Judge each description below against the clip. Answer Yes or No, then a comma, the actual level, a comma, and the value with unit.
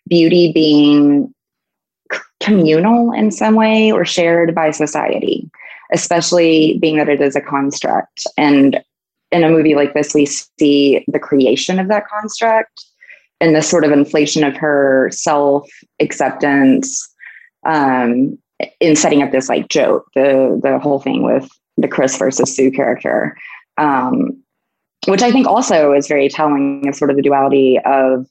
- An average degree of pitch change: Yes, average, 3.8 semitones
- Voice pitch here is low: No, medium, 150 Hz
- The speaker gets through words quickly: No, average, 150 wpm